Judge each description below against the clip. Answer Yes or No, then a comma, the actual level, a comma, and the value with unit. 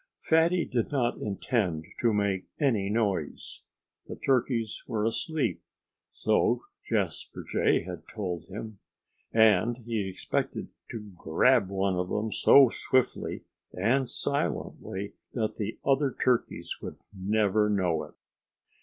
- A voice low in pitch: Yes, low, 110 Hz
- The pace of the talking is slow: Yes, slow, 120 wpm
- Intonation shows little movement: No, average, 4.1 semitones